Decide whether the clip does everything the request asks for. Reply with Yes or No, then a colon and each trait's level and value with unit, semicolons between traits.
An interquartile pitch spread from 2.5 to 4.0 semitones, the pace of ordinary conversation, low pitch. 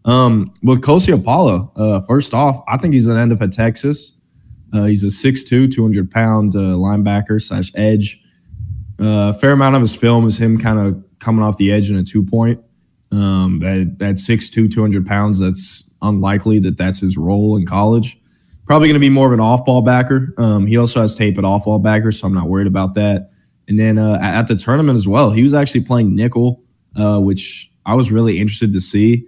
No: average, 3.0 semitones; fast, 215 wpm; low, 110 Hz